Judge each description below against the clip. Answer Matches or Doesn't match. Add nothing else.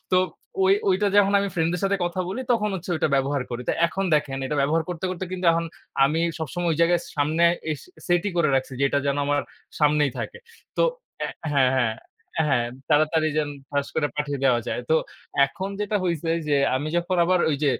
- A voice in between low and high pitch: Matches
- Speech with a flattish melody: Doesn't match